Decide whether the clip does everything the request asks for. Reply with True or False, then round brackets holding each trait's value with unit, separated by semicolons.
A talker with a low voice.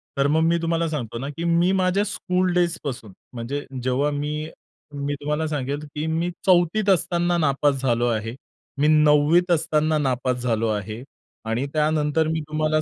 False (150 Hz)